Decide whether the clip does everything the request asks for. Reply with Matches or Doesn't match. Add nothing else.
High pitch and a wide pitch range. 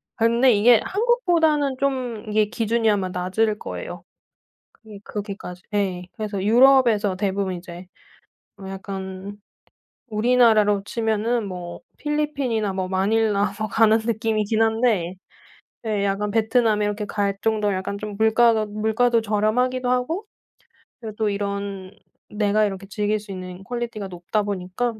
Doesn't match